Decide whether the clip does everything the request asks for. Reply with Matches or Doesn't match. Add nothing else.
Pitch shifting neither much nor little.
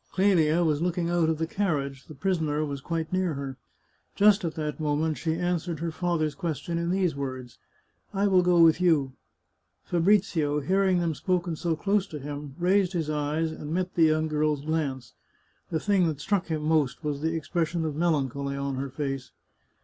Matches